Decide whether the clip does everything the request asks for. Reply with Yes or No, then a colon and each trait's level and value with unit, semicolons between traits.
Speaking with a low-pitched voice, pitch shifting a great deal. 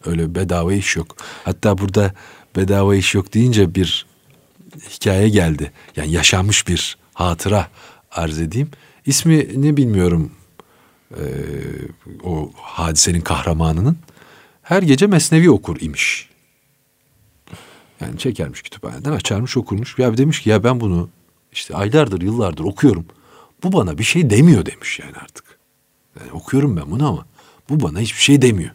Yes: low, 100 Hz; wide, 7.9 semitones